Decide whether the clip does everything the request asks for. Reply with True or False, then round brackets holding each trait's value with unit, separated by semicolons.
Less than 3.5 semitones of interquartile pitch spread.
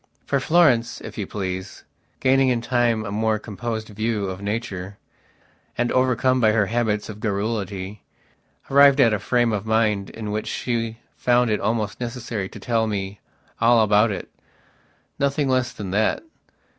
True (2.8 semitones)